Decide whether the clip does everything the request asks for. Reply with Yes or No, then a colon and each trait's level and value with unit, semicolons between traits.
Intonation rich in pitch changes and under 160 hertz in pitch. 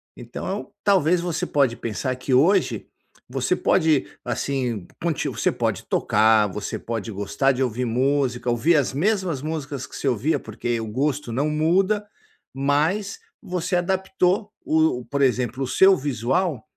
Yes: wide, 5.9 semitones; medium, 140 Hz